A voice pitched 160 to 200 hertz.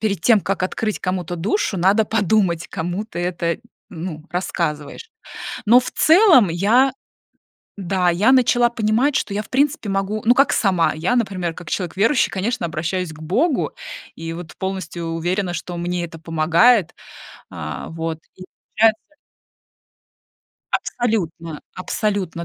Yes: high, 190 Hz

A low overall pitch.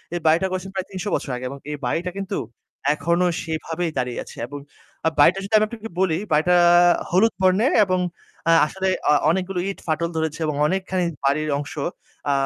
No: medium, 175 Hz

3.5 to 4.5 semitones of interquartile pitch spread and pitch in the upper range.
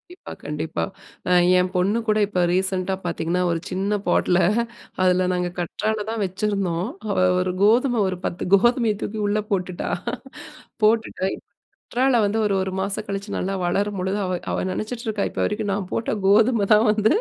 No: average, 2.8 semitones; high, 200 Hz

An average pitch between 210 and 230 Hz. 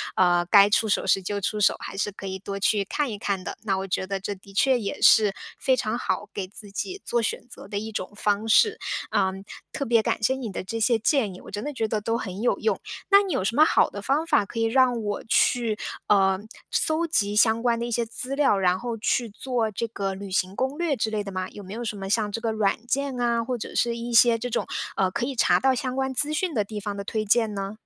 Yes: high, 220 Hz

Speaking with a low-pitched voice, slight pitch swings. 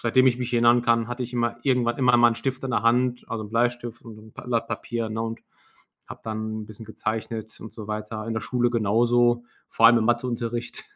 Yes: low, 120 Hz; narrow, 1.5 semitones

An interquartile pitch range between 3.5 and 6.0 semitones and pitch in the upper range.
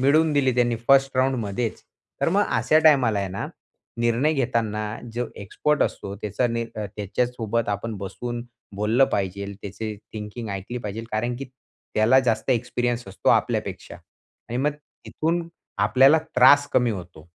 No: average, 3.9 semitones; low, 120 Hz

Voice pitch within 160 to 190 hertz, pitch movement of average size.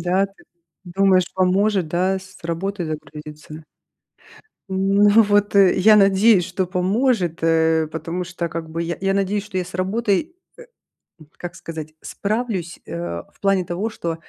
Yes: medium, 185 Hz; average, 3.0 semitones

